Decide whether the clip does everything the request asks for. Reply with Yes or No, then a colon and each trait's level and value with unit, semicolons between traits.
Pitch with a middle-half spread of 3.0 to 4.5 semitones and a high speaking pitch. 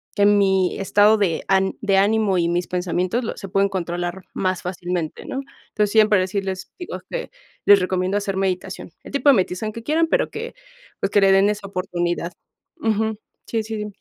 No: narrow, 2.6 semitones; high, 195 Hz